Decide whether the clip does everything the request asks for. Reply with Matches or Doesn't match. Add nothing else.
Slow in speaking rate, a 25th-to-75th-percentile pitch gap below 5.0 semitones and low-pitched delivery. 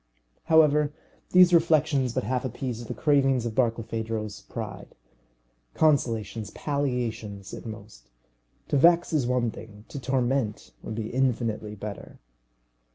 Matches